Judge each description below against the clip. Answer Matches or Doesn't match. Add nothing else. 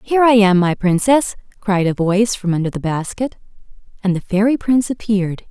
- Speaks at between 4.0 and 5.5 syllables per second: Doesn't match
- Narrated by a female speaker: Matches